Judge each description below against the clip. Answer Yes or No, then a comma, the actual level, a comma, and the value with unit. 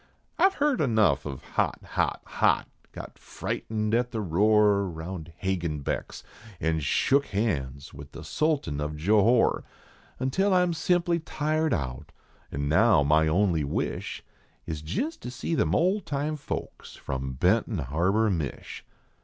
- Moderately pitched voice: No, low, 100 Hz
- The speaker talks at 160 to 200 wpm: No, average, 145 wpm